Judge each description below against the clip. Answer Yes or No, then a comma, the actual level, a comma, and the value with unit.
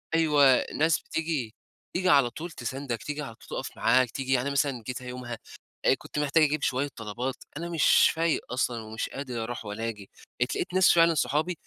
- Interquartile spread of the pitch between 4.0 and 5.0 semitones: Yes, average, 4.3 semitones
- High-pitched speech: No, low, 135 Hz